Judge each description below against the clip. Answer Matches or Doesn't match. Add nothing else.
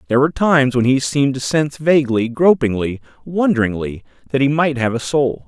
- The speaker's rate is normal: Matches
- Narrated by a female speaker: Doesn't match